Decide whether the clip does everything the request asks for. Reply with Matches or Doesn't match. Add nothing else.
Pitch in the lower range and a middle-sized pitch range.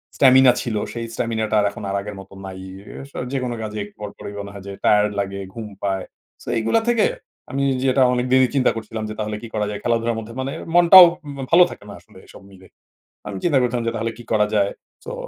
Matches